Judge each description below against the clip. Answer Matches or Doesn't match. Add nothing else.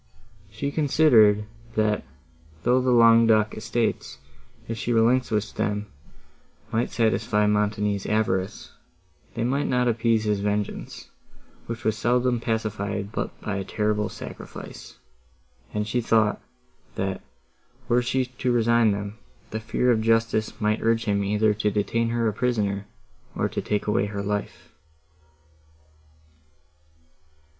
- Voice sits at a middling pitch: Doesn't match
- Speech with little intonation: Matches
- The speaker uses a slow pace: Matches